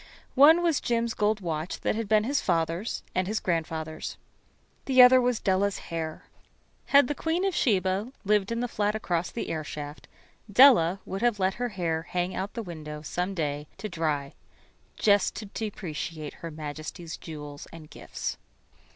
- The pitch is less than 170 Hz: No, high, 190 Hz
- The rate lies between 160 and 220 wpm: Yes, average, 170 wpm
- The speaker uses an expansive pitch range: Yes, wide, 5.8 semitones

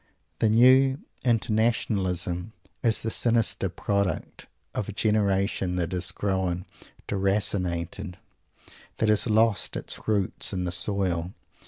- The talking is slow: Yes, slow, 120 wpm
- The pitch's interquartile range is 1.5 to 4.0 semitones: Yes, average, 3.2 semitones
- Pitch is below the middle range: Yes, low, 100 Hz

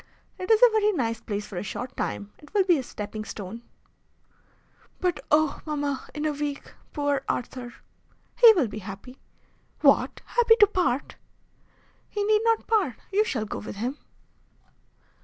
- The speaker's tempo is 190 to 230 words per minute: No, average, 160 wpm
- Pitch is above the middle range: Yes, very high, 285 Hz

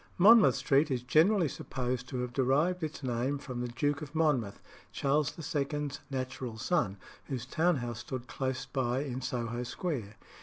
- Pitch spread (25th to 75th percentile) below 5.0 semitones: Yes, average, 3.4 semitones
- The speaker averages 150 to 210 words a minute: Yes, average, 160 wpm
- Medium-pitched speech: No, low, 130 Hz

